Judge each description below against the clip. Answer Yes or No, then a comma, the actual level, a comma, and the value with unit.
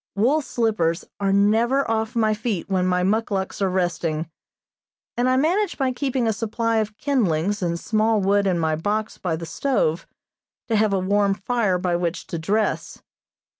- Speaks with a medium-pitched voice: No, high, 205 Hz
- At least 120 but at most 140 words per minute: No, average, 170 wpm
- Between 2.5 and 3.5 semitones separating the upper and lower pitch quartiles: No, average, 3.9 semitones